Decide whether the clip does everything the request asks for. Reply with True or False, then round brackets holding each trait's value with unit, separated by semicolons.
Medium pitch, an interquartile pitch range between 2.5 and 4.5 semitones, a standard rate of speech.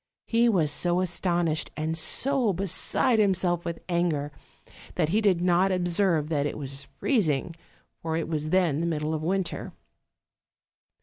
True (170 Hz; 3.3 semitones; 145 wpm)